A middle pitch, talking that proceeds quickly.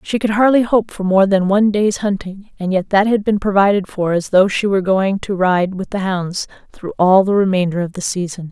No: high, 195 Hz; fast, 240 wpm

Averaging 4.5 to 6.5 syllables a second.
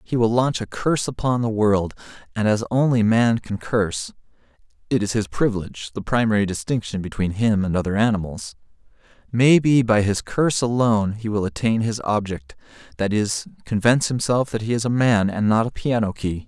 No: 4.0 syllables/s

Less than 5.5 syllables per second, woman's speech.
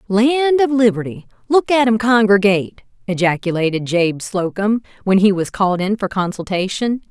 Yes: 5.0 syllables/s; female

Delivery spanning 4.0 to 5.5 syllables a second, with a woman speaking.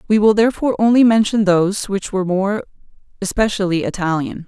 No: 6.3 syllables/s; female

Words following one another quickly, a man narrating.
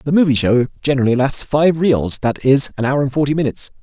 Yes: fast, 220 wpm; male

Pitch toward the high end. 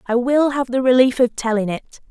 Yes: high, 245 Hz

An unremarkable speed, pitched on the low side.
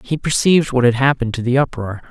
No: fast, 230 wpm; low, 130 Hz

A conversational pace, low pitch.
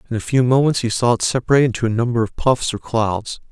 No: fast, 255 wpm; low, 120 Hz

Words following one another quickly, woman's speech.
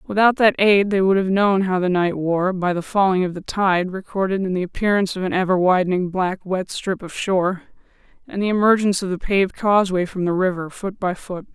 Yes: fast, 225 wpm; female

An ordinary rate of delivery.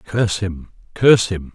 Yes: average, 155 wpm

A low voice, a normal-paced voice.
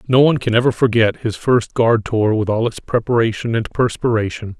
Yes: low, 115 Hz; average, 195 wpm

